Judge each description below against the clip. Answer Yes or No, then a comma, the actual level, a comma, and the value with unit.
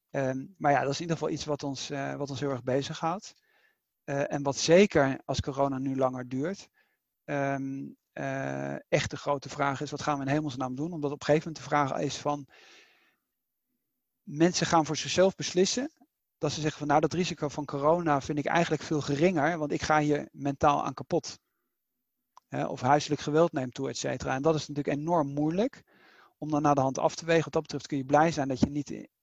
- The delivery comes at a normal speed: No, fast, 220 wpm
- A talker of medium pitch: Yes, medium, 145 Hz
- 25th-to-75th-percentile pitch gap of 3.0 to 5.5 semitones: No, narrow, 2.5 semitones